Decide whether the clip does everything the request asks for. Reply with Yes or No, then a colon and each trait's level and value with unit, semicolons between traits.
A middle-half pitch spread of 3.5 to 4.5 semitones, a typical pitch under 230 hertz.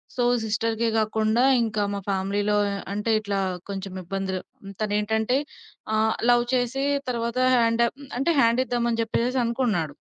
No: narrow, 2.5 semitones; high, 220 Hz